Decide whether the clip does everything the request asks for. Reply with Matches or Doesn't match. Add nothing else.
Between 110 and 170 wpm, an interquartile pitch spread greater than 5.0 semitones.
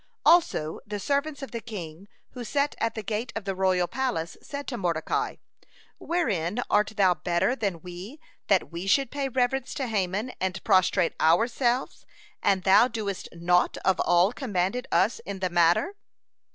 Matches